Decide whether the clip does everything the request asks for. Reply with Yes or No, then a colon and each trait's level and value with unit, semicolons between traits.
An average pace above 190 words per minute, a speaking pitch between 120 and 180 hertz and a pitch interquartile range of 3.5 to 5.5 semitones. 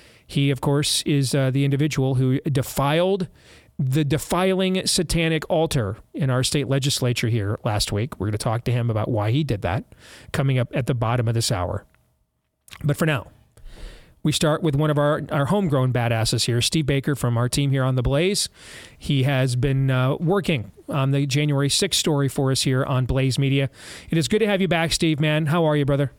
Yes: fast, 205 wpm; medium, 140 Hz; average, 3.8 semitones